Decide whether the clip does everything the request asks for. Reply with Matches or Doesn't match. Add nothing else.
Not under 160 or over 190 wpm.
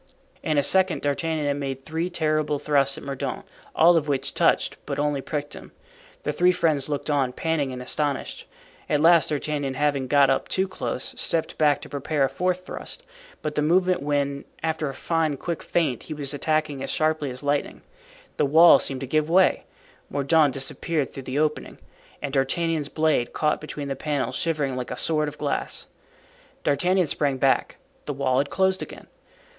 Matches